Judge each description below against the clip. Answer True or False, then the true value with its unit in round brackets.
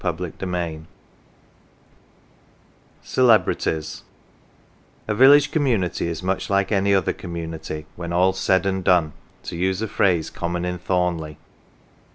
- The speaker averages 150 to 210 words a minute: False (135 wpm)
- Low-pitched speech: True (90 Hz)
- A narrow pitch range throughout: True (2.3 semitones)